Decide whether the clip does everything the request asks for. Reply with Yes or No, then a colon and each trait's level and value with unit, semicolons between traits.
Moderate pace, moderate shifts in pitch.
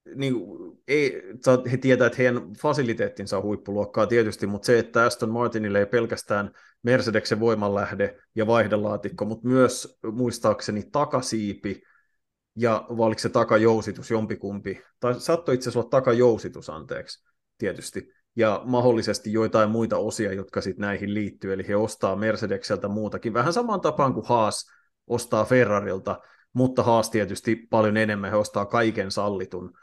Yes: average, 135 wpm; average, 3.0 semitones